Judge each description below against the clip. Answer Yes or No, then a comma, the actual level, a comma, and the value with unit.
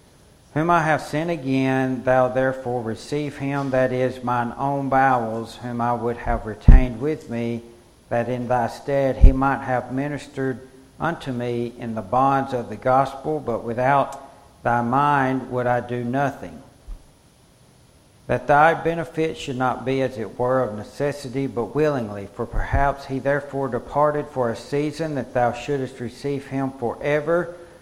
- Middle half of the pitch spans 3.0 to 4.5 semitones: No, narrow, 2.6 semitones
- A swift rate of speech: No, average, 155 wpm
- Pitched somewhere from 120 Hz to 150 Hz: Yes, low, 130 Hz